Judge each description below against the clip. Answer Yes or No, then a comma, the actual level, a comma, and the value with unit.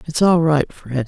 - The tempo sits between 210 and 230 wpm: Yes, fast, 225 wpm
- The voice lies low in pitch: No, medium, 150 Hz